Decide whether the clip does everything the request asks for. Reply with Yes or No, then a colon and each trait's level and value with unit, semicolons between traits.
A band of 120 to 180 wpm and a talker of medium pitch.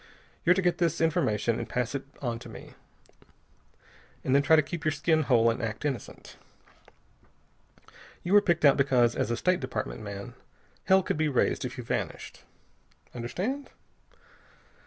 Yes: average, 155 wpm; medium, 145 Hz